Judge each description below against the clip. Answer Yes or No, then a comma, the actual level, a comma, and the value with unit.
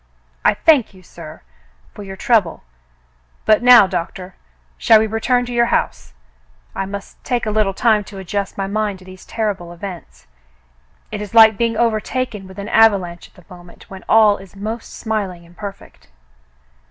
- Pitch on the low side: No, high, 200 Hz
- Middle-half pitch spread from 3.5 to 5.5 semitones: No, average, 3.0 semitones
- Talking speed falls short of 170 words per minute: No, average, 175 wpm